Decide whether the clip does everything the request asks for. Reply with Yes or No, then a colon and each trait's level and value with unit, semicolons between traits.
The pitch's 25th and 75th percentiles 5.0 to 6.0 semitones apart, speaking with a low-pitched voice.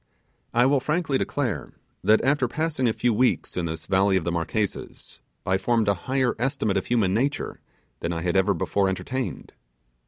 Yes: wide, 5.6 semitones; low, 110 Hz